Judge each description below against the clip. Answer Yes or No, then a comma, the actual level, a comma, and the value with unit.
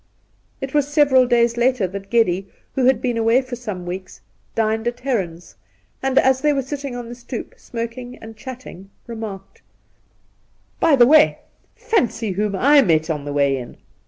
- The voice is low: No, high, 235 Hz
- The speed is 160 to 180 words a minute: Yes, average, 175 wpm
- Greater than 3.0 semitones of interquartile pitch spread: Yes, average, 5.0 semitones